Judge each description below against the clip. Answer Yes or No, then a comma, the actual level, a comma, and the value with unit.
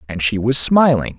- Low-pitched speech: Yes, low, 120 Hz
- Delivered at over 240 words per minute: No, average, 200 wpm